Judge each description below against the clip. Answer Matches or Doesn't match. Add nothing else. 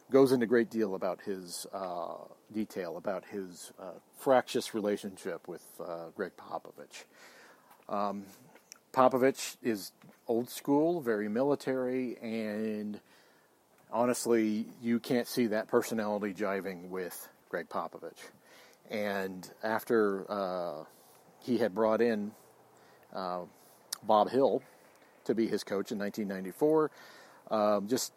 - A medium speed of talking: Doesn't match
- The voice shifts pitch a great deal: Doesn't match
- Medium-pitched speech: Doesn't match